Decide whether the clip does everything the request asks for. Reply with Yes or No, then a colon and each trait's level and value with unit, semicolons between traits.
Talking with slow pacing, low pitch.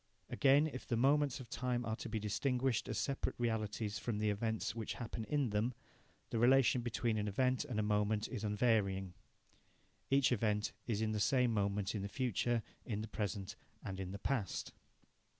No: average, 185 wpm; low, 110 Hz